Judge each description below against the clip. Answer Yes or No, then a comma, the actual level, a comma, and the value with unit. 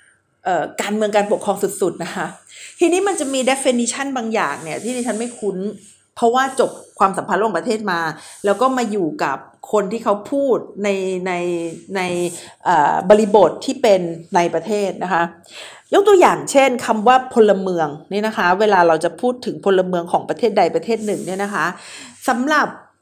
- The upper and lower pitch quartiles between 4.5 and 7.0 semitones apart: Yes, average, 5.2 semitones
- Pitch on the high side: Yes, high, 205 Hz